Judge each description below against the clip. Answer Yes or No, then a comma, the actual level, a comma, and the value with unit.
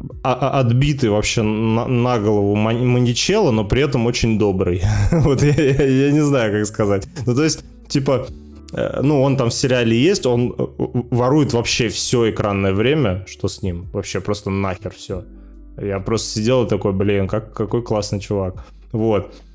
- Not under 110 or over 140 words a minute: No, average, 155 wpm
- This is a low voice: Yes, low, 110 Hz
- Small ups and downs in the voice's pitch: No, average, 4.0 semitones